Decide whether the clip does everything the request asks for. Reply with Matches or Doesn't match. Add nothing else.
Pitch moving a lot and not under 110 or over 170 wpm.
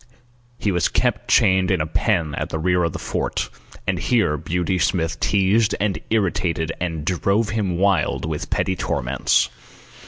Doesn't match